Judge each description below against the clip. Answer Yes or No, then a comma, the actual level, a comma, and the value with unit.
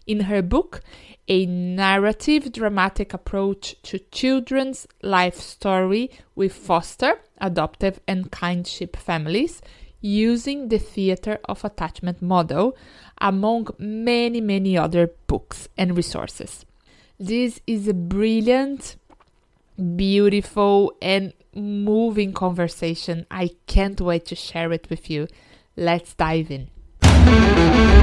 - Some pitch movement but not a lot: Yes, average, 3.5 semitones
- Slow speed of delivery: Yes, slow, 105 wpm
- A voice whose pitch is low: No, high, 195 Hz